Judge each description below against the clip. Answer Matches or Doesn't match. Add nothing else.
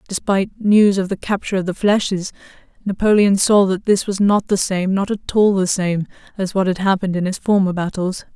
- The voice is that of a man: Doesn't match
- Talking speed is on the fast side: Matches